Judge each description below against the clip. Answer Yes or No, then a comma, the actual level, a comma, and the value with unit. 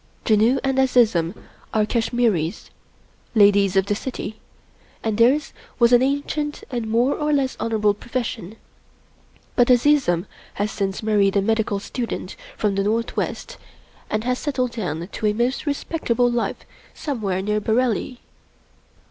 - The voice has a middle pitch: No, high, 225 Hz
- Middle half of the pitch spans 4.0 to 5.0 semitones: No, average, 3.6 semitones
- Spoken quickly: No, average, 140 wpm